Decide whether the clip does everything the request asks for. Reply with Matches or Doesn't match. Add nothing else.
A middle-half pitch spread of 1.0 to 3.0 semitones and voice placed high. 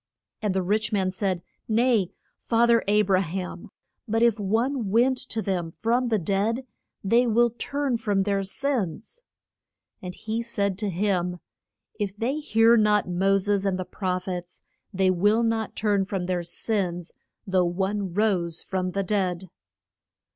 Doesn't match